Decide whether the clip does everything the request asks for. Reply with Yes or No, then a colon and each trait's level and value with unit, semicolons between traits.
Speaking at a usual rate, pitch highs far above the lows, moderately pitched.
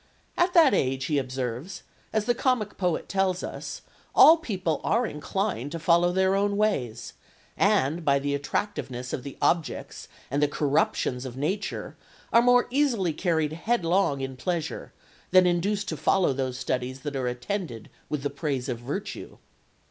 Yes: average, 160 wpm; wide, 6.7 semitones; medium, 165 Hz